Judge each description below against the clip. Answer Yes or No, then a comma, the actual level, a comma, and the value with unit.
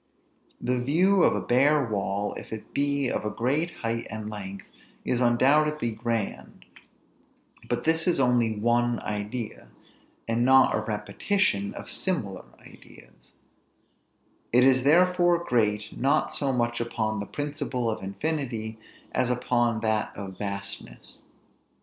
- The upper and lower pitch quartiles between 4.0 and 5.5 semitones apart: Yes, average, 4.7 semitones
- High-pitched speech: No, low, 120 Hz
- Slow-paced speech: Yes, slow, 130 wpm